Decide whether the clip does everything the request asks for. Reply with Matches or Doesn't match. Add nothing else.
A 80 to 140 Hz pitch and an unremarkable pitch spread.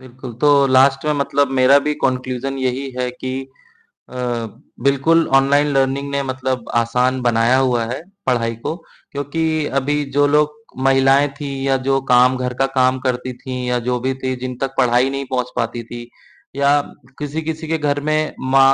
Doesn't match